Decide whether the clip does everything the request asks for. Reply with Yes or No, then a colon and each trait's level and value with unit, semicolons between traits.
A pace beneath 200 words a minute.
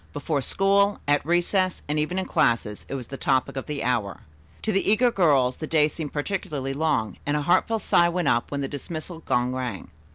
No: fast, 205 wpm